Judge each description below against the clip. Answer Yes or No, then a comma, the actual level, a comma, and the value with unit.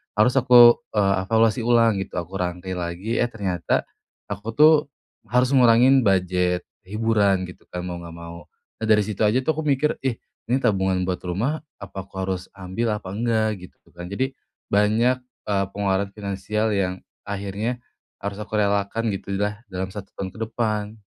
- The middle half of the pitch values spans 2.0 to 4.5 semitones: Yes, average, 3.4 semitones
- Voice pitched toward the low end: Yes, low, 105 Hz